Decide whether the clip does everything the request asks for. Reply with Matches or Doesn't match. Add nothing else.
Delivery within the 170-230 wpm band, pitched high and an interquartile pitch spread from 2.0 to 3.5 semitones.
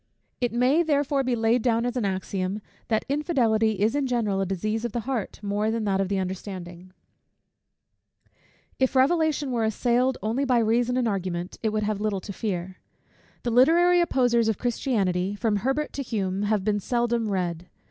Doesn't match